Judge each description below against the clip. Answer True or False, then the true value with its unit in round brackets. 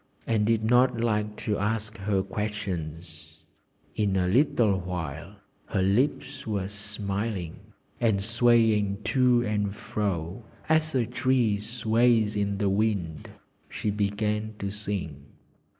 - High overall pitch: False (105 Hz)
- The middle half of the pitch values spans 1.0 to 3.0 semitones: True (2.5 semitones)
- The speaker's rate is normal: False (125 wpm)